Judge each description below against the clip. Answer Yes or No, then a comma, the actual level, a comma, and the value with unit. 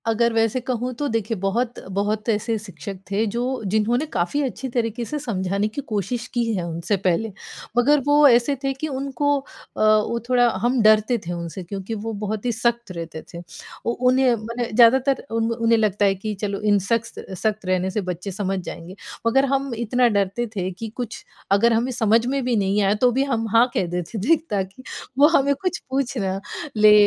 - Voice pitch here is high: Yes, high, 225 Hz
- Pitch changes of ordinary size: Yes, average, 3.7 semitones